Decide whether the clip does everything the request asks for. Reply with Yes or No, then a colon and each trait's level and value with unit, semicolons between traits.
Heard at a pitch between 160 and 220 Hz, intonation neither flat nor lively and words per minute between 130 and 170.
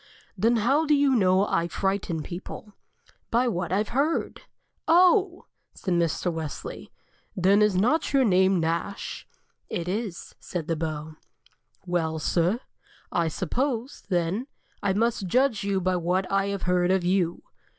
Yes: high, 190 Hz; average, 5.0 semitones; average, 150 wpm